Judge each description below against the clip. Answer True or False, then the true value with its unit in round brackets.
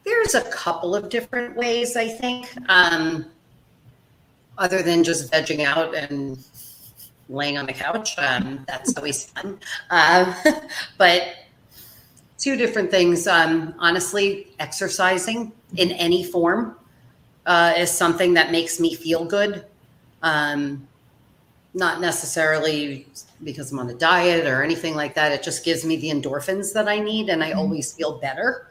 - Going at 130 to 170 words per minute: True (140 wpm)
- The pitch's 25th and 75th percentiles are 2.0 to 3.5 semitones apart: False (4.6 semitones)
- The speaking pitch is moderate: True (165 Hz)